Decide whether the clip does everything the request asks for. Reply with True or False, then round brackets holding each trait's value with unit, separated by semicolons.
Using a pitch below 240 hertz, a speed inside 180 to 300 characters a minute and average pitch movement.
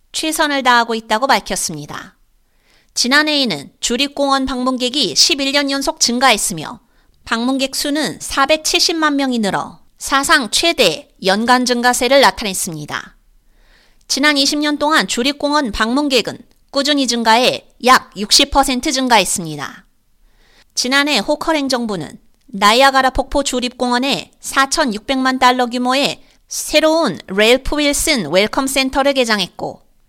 False (265 Hz; 260 characters per minute; 3.5 semitones)